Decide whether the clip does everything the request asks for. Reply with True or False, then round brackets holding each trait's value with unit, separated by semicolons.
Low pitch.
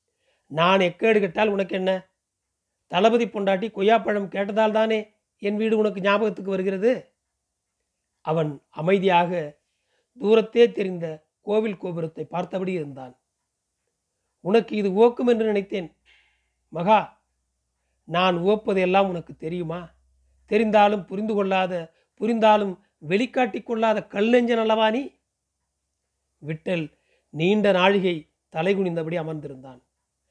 False (190 Hz)